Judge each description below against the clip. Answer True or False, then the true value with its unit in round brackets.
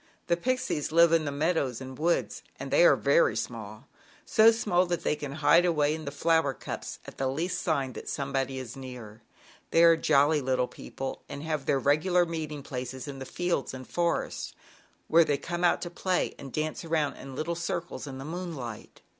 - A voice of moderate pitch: True (155 Hz)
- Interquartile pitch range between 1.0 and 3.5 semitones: False (4.1 semitones)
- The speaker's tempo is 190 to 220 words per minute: True (195 wpm)